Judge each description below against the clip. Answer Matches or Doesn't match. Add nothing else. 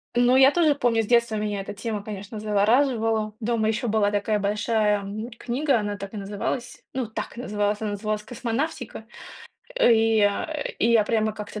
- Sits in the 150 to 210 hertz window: Doesn't match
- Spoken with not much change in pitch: Matches